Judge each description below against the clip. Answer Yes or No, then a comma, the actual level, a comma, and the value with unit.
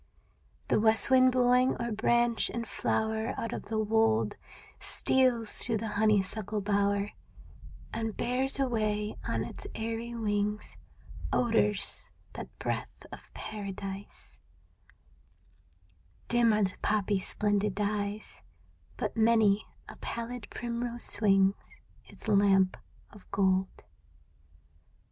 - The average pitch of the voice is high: Yes, high, 215 Hz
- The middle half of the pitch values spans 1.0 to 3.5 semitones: Yes, narrow, 2.4 semitones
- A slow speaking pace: Yes, slow, 110 wpm